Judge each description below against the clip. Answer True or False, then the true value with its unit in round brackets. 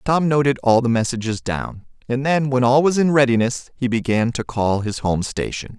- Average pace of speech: False (210 wpm)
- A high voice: False (125 Hz)